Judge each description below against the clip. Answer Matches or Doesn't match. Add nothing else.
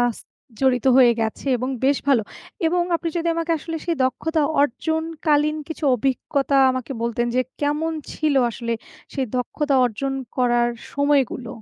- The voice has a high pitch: Matches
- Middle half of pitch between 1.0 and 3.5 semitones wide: Doesn't match